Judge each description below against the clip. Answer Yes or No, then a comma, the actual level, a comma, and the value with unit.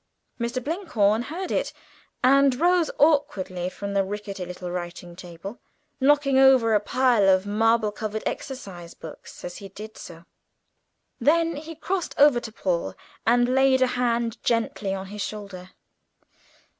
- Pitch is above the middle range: Yes, high, 225 Hz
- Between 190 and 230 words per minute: No, average, 145 wpm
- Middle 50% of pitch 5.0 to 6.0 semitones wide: Yes, wide, 5.5 semitones